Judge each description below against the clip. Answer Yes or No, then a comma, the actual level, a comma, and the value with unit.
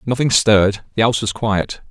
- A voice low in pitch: Yes, low, 110 Hz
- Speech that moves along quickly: No, average, 155 wpm